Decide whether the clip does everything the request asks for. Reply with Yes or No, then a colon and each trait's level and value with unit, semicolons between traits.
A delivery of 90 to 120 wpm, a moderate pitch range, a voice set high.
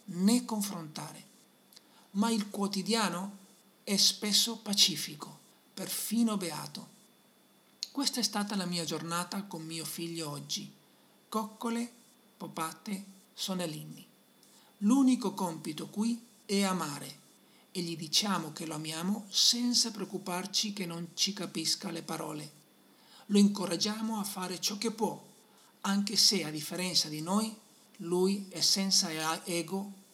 Yes: slow, 115 wpm; average, 4.0 semitones; high, 195 Hz